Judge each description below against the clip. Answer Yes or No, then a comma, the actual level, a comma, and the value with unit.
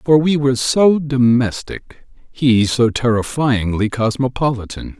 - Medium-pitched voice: No, low, 125 Hz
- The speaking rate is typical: No, slow, 110 wpm